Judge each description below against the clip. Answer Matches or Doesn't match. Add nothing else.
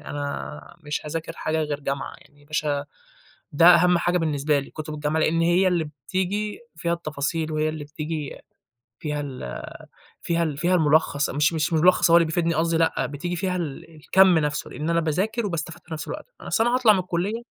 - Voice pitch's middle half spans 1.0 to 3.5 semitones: Matches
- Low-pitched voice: Doesn't match